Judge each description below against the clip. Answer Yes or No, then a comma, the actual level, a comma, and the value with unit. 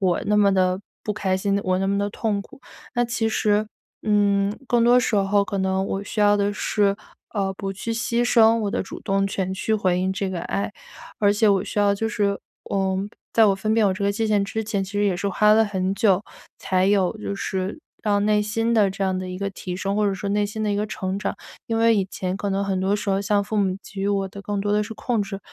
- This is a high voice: Yes, high, 200 Hz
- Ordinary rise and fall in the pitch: No, narrow, 1.6 semitones